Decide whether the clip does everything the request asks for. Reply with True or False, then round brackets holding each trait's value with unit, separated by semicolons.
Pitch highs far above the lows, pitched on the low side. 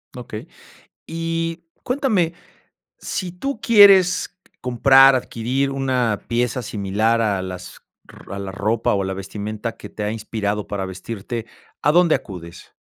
True (8.1 semitones; 115 Hz)